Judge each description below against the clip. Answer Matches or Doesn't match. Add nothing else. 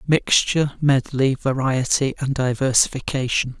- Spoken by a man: Matches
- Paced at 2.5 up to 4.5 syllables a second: Matches